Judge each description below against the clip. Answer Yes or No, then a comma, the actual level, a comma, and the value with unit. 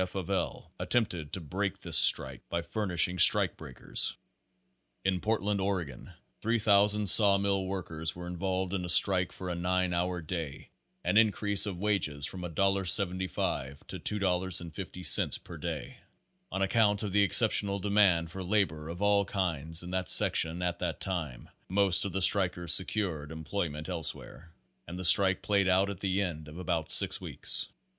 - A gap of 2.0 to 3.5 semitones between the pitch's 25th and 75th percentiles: Yes, average, 2.7 semitones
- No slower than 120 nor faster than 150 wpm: No, average, 165 wpm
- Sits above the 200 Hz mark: No, very low, 95 Hz